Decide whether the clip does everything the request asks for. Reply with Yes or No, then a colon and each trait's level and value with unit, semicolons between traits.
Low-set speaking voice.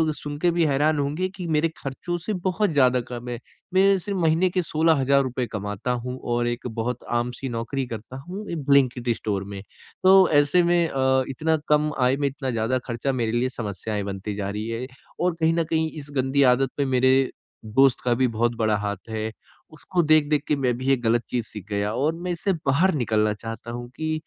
Yes: low, 130 Hz